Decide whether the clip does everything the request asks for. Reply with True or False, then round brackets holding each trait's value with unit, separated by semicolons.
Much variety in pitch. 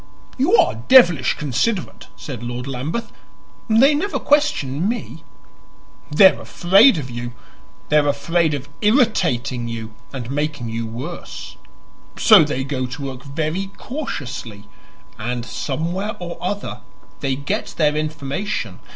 True (7.3 semitones)